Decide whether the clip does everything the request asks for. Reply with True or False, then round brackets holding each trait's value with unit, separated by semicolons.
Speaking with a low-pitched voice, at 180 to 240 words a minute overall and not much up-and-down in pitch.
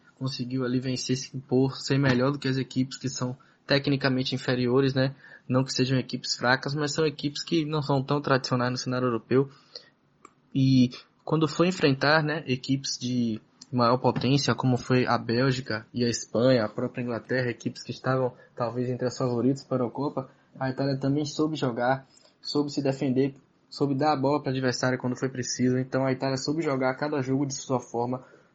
True (130 Hz; 185 wpm; 1.8 semitones)